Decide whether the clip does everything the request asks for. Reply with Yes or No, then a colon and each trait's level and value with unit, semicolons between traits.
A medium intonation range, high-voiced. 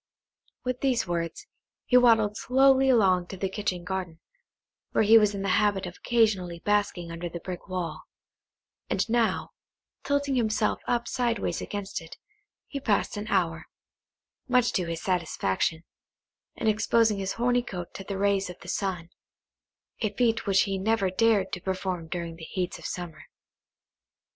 Yes: average, 4.1 semitones; high, 195 Hz